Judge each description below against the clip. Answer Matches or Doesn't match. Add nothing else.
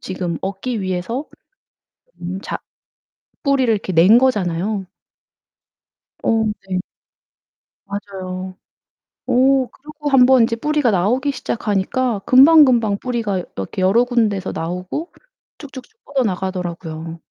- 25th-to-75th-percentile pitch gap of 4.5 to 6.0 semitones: Matches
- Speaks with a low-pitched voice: Doesn't match